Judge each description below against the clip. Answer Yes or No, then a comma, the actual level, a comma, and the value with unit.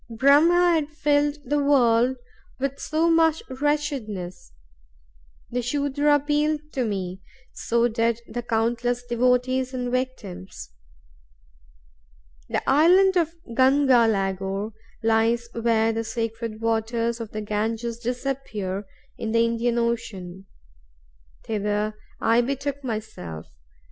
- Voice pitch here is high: Yes, high, 235 Hz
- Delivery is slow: Yes, slow, 110 wpm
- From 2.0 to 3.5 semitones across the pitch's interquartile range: No, average, 4.0 semitones